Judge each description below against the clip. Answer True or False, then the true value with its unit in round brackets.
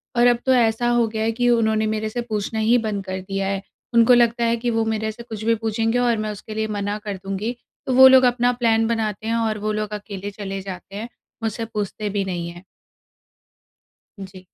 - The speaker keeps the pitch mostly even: True (2.3 semitones)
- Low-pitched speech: False (220 Hz)